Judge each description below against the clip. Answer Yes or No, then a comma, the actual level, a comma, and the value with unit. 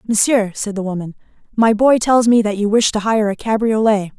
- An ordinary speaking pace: No, fast, 215 wpm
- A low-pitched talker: No, high, 215 Hz